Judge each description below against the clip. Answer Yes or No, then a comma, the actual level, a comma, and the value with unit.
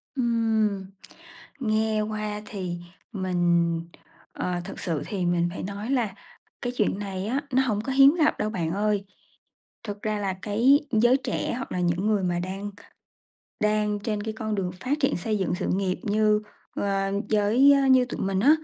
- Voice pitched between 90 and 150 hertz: No, high, 210 Hz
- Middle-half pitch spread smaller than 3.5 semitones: Yes, average, 2.8 semitones